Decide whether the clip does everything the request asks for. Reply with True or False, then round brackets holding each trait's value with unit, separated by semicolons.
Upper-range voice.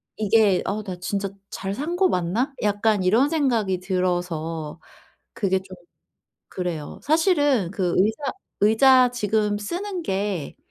True (205 Hz)